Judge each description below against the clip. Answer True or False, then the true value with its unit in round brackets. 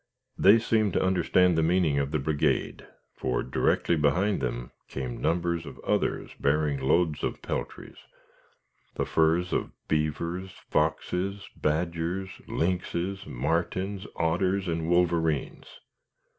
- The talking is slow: True (115 wpm)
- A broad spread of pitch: False (3.3 semitones)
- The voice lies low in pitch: True (85 Hz)